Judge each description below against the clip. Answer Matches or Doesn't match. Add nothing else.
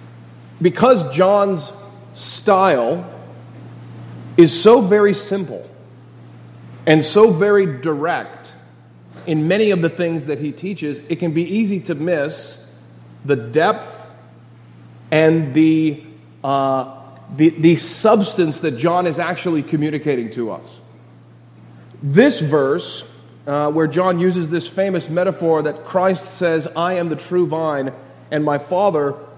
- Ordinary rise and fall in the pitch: Doesn't match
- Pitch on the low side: Doesn't match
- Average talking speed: Doesn't match